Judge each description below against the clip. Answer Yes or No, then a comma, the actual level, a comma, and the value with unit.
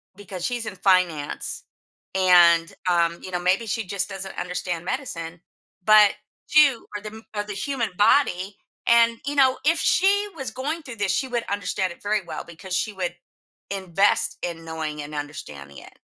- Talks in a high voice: Yes, high, 195 Hz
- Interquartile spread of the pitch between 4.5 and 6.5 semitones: Yes, average, 4.9 semitones